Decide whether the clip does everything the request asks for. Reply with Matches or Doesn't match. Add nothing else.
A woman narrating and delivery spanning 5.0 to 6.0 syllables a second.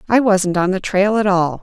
Doesn't match